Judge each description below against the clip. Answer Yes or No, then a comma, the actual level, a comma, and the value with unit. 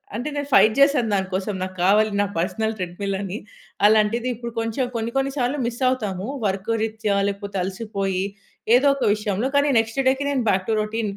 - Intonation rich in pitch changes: No, average, 3.5 semitones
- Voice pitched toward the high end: Yes, high, 215 Hz